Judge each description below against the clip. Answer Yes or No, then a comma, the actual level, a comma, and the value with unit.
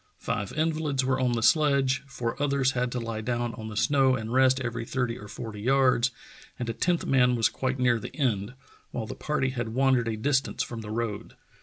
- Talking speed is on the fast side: Yes, fast, 210 wpm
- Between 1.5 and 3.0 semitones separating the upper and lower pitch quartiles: Yes, narrow, 2.6 semitones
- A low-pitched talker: Yes, low, 125 Hz